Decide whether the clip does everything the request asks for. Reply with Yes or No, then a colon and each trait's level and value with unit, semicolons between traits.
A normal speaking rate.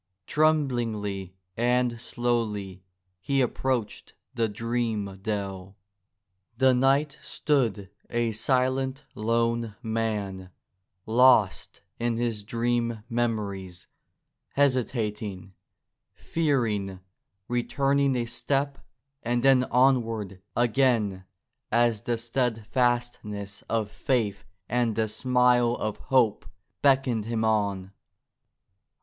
No: slow, 90 wpm